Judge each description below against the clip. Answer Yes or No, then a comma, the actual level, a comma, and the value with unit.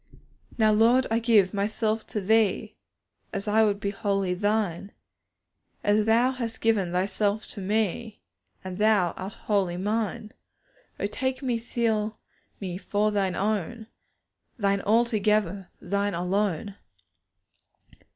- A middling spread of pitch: No, narrow, 2.1 semitones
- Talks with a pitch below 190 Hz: No, high, 210 Hz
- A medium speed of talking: No, slow, 120 wpm